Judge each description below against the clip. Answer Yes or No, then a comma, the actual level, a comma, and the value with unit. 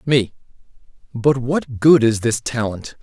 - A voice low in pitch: Yes, low, 120 Hz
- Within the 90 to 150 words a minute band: Yes, average, 140 wpm